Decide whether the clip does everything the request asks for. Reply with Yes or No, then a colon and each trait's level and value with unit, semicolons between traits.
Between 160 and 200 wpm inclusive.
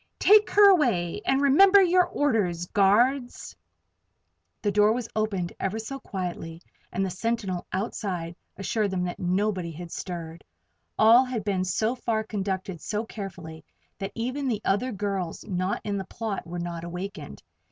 No: average, 150 wpm